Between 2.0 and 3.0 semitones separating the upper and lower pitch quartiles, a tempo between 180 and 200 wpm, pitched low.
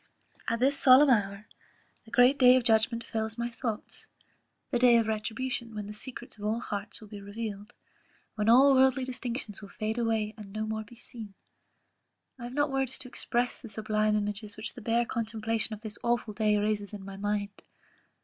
No: narrow, 2.4 semitones; average, 190 wpm; high, 220 Hz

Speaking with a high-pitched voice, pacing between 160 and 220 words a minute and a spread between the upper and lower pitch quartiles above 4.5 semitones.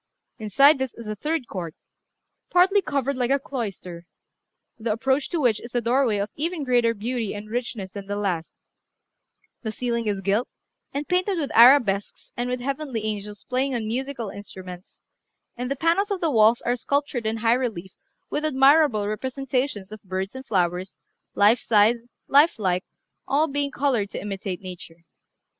Yes: high, 235 Hz; average, 165 wpm; average, 5.1 semitones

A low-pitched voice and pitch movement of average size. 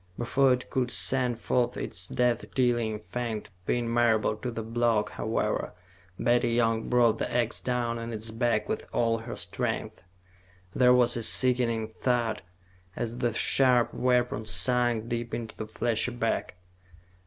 No: low, 120 Hz; narrow, 1.5 semitones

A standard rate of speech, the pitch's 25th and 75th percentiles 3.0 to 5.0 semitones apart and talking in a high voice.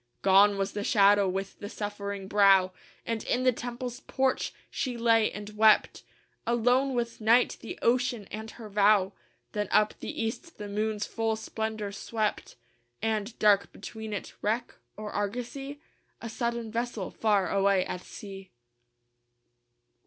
No: average, 145 wpm; narrow, 2.6 semitones; high, 215 Hz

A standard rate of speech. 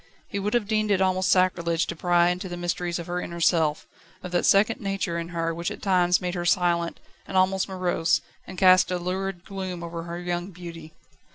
No: fast, 210 wpm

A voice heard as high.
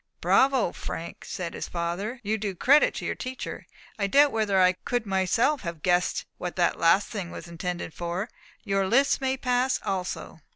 Yes: high, 195 Hz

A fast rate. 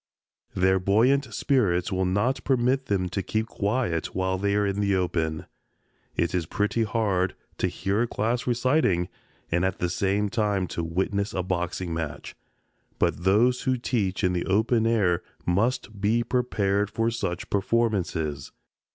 No: average, 155 wpm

